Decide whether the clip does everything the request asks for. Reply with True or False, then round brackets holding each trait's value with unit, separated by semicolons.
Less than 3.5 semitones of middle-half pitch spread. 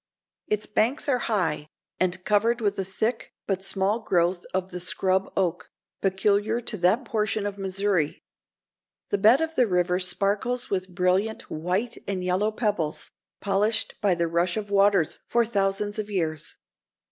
True (2.9 semitones)